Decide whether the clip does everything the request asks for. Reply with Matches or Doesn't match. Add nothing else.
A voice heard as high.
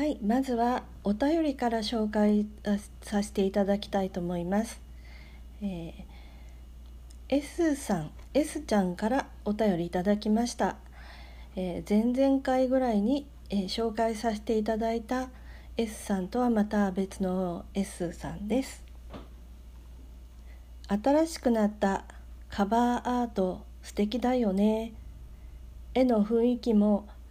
Matches